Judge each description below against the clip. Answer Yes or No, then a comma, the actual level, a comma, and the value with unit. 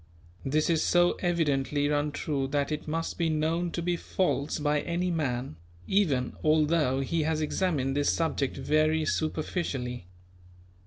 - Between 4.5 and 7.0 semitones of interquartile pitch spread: No, average, 2.8 semitones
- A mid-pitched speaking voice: Yes, medium, 155 Hz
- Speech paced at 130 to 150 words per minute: Yes, average, 140 wpm